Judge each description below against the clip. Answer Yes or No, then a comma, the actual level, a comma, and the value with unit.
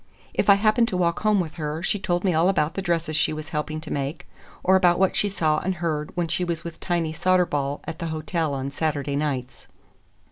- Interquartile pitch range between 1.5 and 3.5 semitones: Yes, average, 3.0 semitones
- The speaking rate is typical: No, fast, 225 wpm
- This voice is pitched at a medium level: Yes, medium, 165 Hz